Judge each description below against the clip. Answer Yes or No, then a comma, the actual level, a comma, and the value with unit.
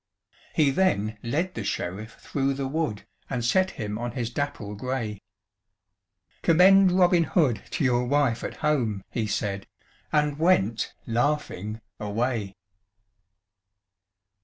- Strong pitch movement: Yes, wide, 5.9 semitones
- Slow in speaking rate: Yes, slow, 120 wpm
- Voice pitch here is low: Yes, low, 125 Hz